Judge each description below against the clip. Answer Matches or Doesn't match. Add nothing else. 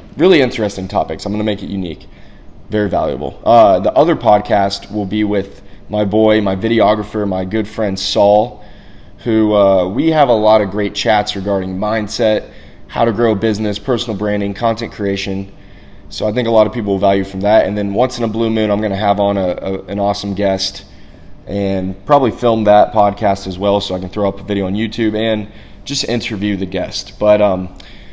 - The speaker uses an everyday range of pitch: Doesn't match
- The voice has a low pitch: Matches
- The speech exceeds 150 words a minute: Matches